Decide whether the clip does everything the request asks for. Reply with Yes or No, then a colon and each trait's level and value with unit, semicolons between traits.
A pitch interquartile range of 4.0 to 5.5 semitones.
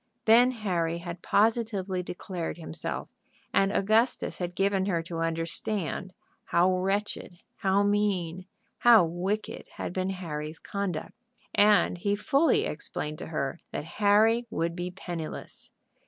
No: average, 3.5 semitones